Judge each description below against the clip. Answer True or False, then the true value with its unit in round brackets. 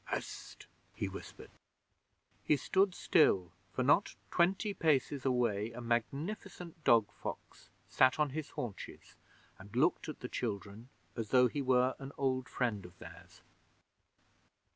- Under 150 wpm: True (135 wpm)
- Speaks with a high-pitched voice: False (130 Hz)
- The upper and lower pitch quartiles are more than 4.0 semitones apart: True (4.8 semitones)